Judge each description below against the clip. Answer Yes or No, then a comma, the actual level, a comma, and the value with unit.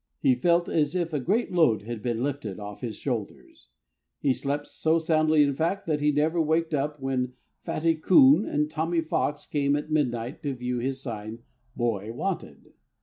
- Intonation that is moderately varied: Yes, average, 4.4 semitones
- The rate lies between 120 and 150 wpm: No, average, 185 wpm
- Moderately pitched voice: Yes, medium, 145 Hz